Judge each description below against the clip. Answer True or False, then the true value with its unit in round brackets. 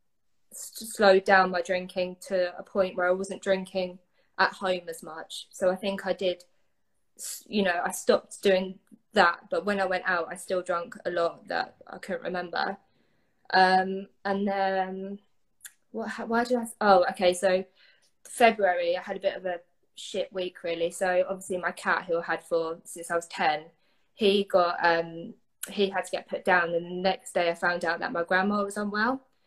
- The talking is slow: False (190 wpm)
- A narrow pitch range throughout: True (2.0 semitones)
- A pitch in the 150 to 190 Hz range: True (185 Hz)